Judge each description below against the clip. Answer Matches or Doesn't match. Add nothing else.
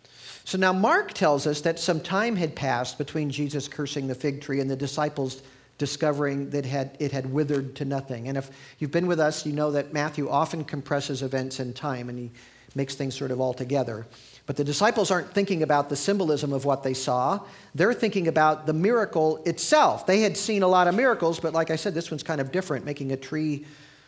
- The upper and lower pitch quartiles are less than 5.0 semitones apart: Matches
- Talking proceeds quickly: Matches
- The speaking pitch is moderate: Matches